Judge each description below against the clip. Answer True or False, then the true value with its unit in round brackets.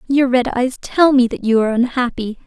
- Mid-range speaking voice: False (250 Hz)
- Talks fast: True (220 wpm)